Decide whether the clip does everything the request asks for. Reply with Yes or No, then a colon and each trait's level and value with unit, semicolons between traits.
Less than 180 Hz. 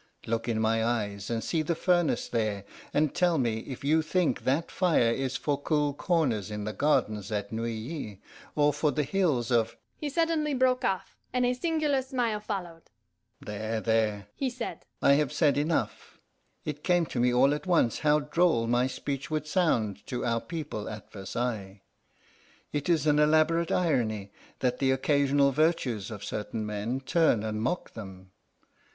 Yes: medium, 140 Hz